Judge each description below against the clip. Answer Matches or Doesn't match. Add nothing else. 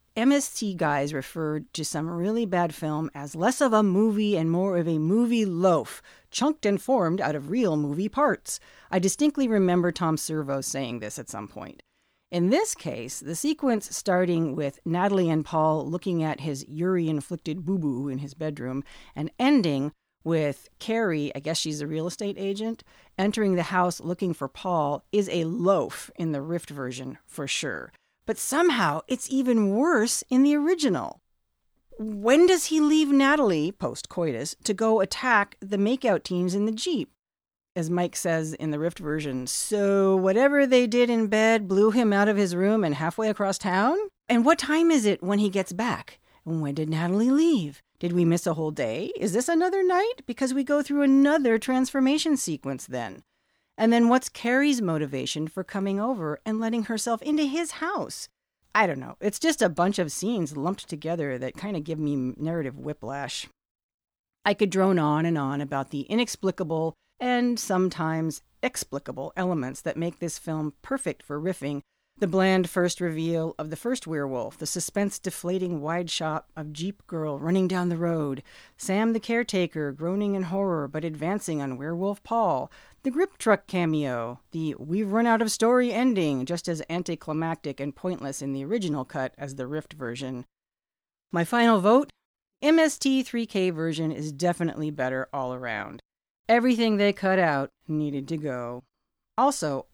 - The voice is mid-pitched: Matches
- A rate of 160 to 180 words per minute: Matches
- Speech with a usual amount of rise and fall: Doesn't match